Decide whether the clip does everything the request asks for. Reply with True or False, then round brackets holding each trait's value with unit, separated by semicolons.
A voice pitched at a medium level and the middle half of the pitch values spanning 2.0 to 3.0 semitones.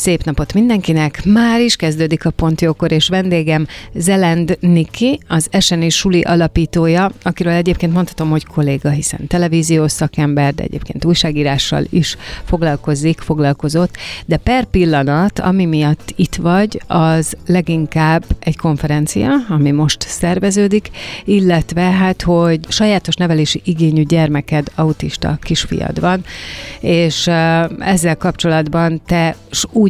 True (165 Hz; 2.5 semitones)